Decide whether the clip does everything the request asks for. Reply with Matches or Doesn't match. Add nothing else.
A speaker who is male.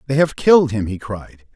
Matches